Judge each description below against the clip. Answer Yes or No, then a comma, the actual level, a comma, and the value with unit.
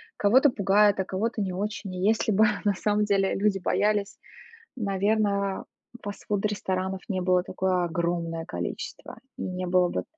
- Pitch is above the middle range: Yes, high, 195 Hz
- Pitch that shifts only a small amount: Yes, narrow, 2.1 semitones